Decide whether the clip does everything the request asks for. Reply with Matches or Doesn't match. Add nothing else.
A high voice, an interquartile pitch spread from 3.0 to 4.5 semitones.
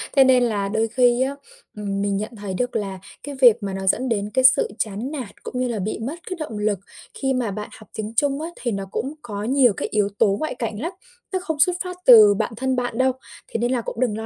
Matches